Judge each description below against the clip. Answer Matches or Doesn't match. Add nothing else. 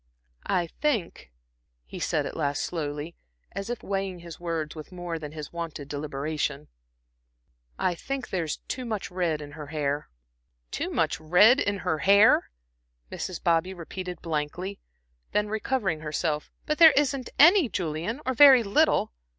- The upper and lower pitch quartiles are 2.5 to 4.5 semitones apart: Doesn't match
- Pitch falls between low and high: Matches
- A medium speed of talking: Matches